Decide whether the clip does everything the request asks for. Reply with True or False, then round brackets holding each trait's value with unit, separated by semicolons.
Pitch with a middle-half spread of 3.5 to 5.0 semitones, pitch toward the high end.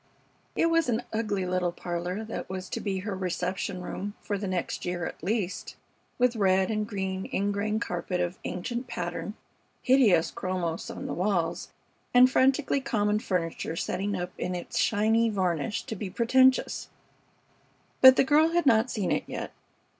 True (4.2 semitones; 200 Hz)